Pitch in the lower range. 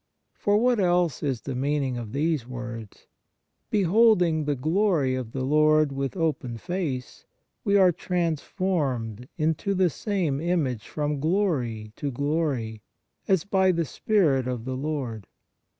No: medium, 150 Hz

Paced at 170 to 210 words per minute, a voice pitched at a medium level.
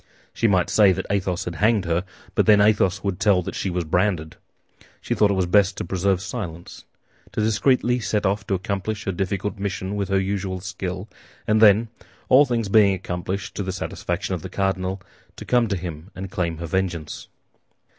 No: average, 195 wpm; very low, 95 Hz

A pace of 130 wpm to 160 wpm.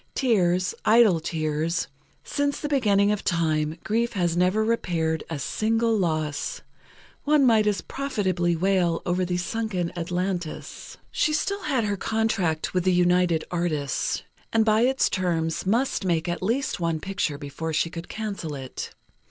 Yes: average, 150 wpm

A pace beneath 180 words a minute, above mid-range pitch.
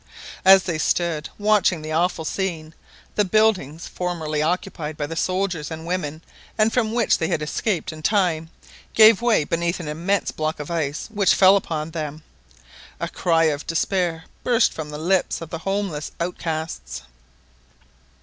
No: average, 160 wpm; medium, 170 Hz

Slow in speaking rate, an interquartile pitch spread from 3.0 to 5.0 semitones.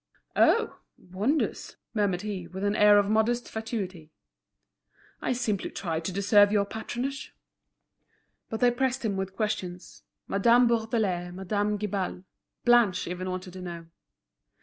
Yes: slow, 130 wpm; average, 3.3 semitones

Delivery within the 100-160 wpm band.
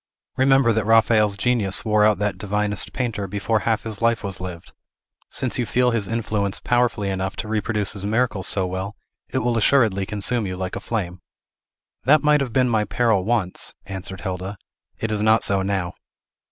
No: average, 180 wpm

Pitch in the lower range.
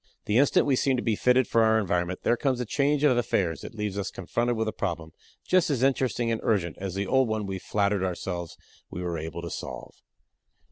Yes: low, 110 Hz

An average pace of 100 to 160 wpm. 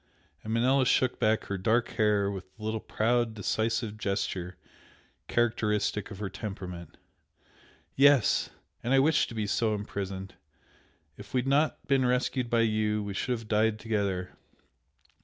Yes: average, 150 wpm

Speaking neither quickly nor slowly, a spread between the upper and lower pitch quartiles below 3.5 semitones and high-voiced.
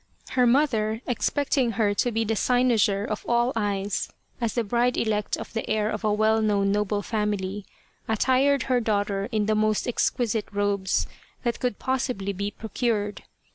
Yes: average, 165 wpm; average, 2.8 semitones; high, 215 Hz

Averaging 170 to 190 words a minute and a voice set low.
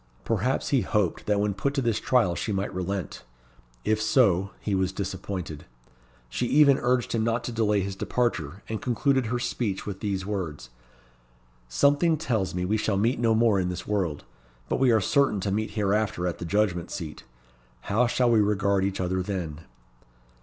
Yes: average, 180 wpm; low, 105 Hz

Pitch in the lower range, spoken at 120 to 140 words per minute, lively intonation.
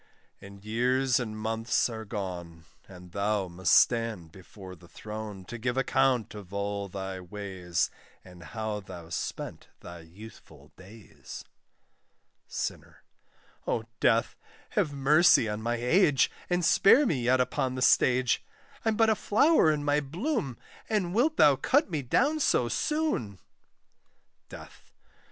Yes: low, 115 Hz; slow, 135 wpm; wide, 6.4 semitones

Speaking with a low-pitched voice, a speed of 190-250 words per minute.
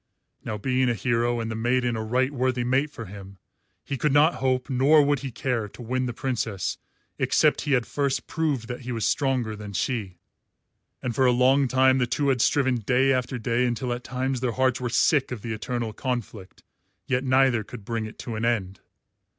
Yes: low, 125 Hz; fast, 205 wpm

